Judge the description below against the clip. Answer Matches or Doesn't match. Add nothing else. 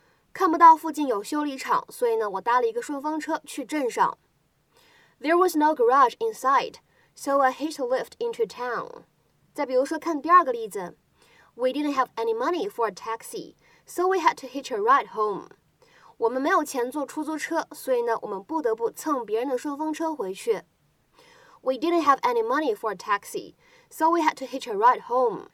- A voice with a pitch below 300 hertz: Doesn't match